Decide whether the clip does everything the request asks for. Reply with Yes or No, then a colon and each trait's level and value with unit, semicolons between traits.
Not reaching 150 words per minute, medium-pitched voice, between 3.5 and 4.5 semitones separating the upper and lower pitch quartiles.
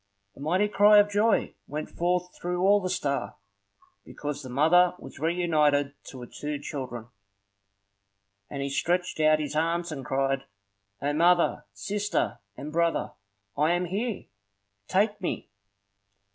Yes: average, 140 wpm; medium, 165 Hz; average, 3.9 semitones